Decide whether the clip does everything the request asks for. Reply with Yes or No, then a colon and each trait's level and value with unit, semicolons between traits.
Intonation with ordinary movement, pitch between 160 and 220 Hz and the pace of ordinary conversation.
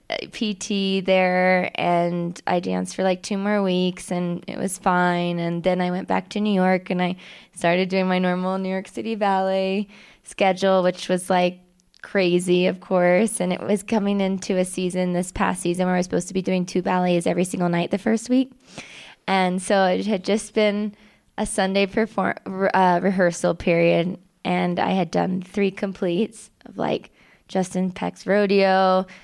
No: narrow, 1.7 semitones; medium, 185 Hz; average, 180 wpm